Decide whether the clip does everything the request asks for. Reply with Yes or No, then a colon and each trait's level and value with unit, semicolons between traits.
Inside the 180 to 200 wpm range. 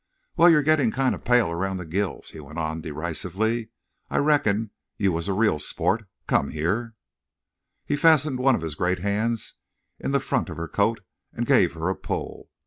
Yes: average, 185 wpm